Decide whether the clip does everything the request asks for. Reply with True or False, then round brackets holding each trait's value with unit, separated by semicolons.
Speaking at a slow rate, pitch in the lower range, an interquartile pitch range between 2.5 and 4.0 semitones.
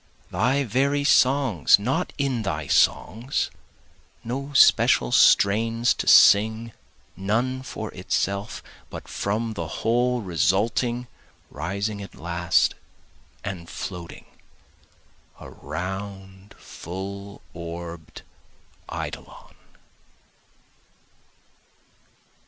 False (80 wpm; 100 Hz; 4.5 semitones)